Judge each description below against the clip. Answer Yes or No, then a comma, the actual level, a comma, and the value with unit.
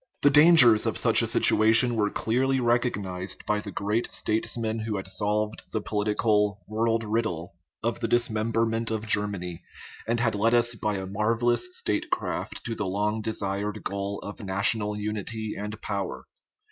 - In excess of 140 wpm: Yes, average, 170 wpm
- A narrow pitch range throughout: Yes, narrow, 2.0 semitones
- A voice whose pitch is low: Yes, low, 110 Hz